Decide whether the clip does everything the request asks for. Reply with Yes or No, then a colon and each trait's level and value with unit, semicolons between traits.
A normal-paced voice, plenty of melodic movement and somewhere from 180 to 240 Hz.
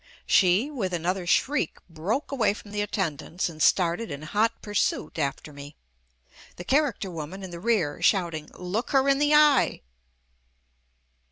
Yes: average, 165 wpm; wide, 5.8 semitones; high, 190 Hz